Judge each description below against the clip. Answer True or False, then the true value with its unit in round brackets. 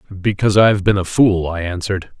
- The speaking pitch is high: False (95 Hz)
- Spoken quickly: True (220 wpm)